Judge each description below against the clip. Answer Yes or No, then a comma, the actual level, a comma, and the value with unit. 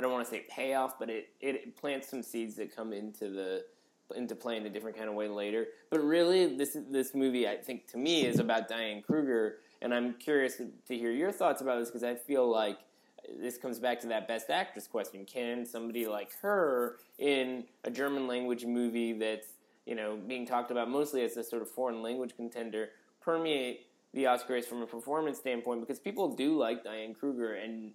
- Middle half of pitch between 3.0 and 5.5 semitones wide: No, narrow, 2.5 semitones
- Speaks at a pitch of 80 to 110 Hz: No, low, 120 Hz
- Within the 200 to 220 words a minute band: Yes, fast, 205 wpm